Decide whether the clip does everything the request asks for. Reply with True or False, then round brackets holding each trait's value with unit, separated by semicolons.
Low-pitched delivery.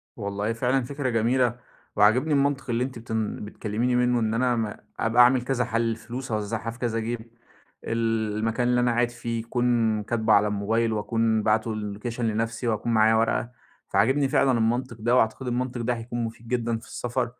True (115 Hz)